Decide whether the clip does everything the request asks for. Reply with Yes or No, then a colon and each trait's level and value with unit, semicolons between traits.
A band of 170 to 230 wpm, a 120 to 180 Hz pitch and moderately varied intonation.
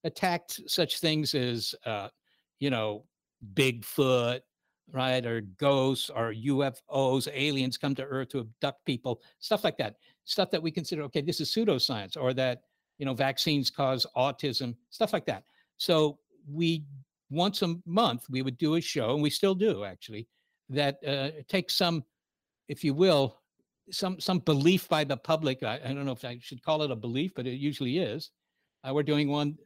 Yes: average, 180 wpm; medium, 140 Hz; average, 3.6 semitones